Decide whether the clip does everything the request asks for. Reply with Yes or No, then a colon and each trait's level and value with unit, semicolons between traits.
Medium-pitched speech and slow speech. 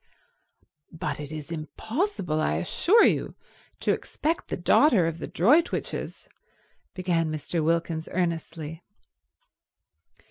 Yes: medium, 165 Hz; slow, 105 wpm